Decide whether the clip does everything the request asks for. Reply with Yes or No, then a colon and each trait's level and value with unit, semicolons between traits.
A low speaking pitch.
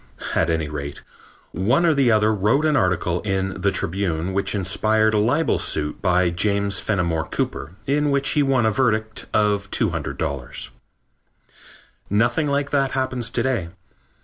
Yes: low, 105 Hz